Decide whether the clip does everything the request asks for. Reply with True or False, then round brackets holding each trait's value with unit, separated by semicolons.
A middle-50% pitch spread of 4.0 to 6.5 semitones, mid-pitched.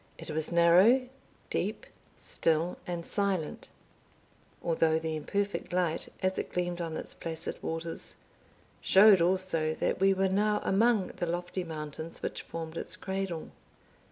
False (2.9 semitones; 175 Hz)